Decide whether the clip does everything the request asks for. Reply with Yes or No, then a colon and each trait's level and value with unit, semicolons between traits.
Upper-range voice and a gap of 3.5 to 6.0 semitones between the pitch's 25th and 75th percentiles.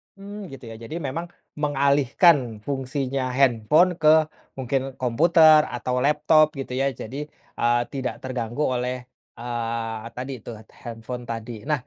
No: low, 130 Hz; average, 3.9 semitones